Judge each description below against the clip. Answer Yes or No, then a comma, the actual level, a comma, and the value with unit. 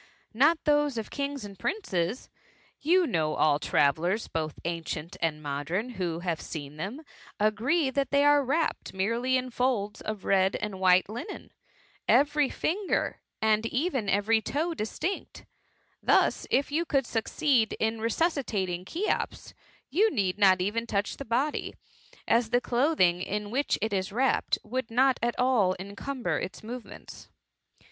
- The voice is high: Yes, high, 225 Hz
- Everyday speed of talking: Yes, average, 150 wpm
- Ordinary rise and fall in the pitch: No, wide, 6.6 semitones